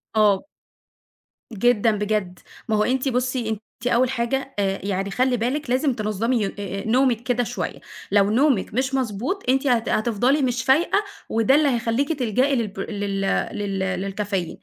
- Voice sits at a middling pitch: No, high, 230 Hz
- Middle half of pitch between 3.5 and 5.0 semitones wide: Yes, average, 4.1 semitones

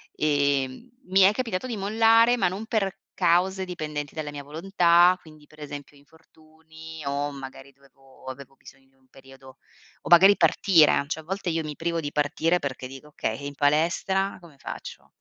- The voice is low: No, medium, 155 Hz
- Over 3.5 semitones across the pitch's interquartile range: Yes, average, 4.5 semitones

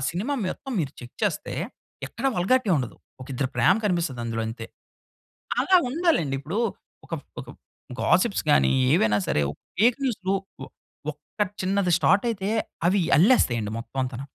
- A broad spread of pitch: Yes, wide, 8.7 semitones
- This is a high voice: No, medium, 180 Hz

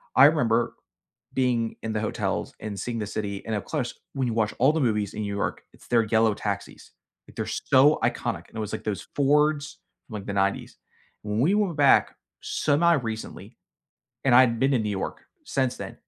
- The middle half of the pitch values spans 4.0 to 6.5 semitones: Yes, average, 4.6 semitones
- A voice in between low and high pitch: No, low, 115 Hz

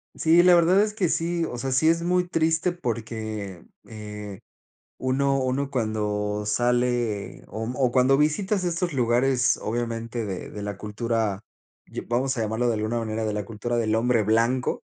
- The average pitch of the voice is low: Yes, low, 120 Hz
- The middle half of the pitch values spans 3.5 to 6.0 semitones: Yes, average, 4.4 semitones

